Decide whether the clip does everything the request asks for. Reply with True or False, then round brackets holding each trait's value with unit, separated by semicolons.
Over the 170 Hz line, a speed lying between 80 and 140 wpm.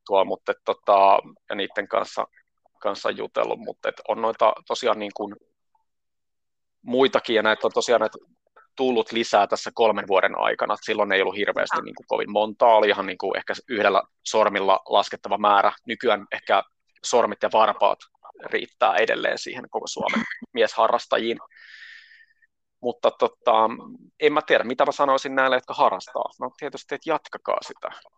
False (190 Hz; 150 wpm)